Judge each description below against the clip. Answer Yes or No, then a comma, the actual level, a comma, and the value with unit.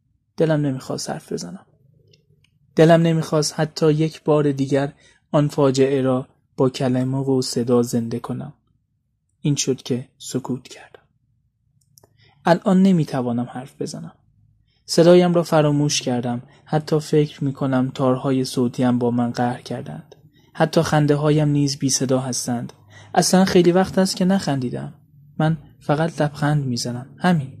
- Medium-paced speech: Yes, average, 130 wpm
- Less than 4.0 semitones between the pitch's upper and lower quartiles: Yes, average, 3.3 semitones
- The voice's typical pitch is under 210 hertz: Yes, medium, 140 Hz